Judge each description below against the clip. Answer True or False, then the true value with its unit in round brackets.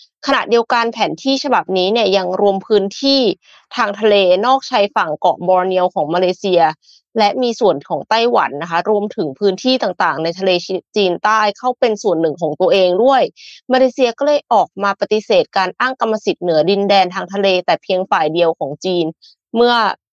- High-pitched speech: True (200 Hz)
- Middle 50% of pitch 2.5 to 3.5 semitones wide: False (4.2 semitones)